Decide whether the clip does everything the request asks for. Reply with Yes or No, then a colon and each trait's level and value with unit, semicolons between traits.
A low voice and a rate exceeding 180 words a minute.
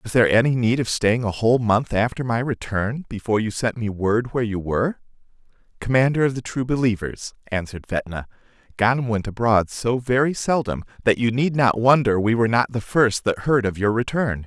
Yes: low, 115 Hz; average, 200 wpm